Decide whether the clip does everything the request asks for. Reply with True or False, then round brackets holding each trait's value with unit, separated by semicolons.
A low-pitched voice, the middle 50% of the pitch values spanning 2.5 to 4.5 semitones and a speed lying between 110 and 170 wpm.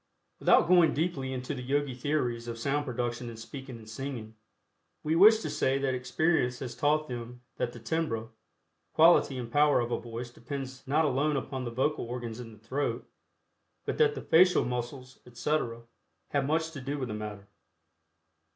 False (130 Hz; 3.6 semitones; 180 wpm)